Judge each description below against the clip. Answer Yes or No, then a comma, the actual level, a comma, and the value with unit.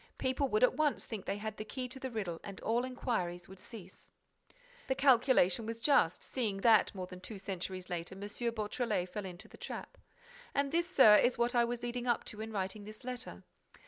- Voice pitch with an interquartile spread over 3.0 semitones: Yes, average, 4.4 semitones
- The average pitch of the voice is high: Yes, high, 220 Hz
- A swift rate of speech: Yes, fast, 210 wpm